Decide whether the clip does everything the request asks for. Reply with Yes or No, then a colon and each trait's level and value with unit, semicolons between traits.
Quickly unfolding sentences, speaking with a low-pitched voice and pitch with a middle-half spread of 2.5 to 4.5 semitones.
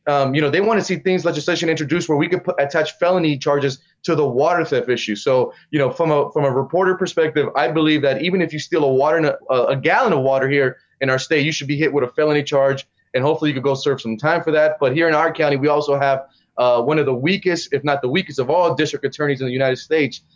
No: fast, 270 wpm; medium, 150 Hz; average, 3.2 semitones